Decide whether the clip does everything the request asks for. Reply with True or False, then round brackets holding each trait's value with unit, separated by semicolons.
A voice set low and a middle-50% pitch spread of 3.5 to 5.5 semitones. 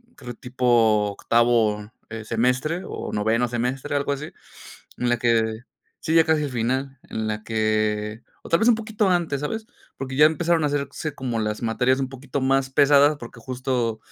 True (125 Hz; 4.1 semitones)